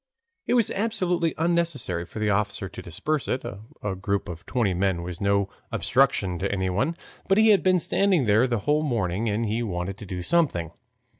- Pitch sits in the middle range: No, low, 105 Hz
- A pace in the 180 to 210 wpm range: Yes, average, 190 wpm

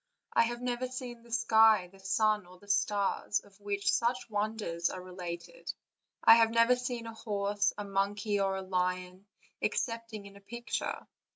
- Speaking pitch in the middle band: No, high, 205 Hz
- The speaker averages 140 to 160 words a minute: No, average, 170 wpm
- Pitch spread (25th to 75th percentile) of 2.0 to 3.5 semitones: Yes, average, 3.0 semitones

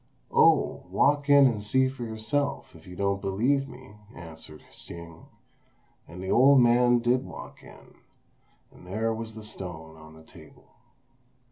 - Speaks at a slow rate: No, average, 150 wpm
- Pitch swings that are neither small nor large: No, wide, 6.5 semitones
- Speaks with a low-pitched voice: Yes, low, 110 Hz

